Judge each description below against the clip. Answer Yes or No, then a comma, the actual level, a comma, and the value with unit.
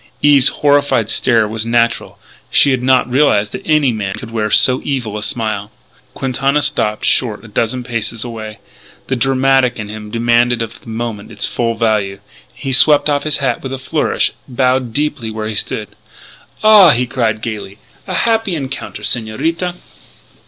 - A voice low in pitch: Yes, low, 120 Hz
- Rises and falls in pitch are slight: No, average, 3.7 semitones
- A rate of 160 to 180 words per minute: Yes, average, 165 wpm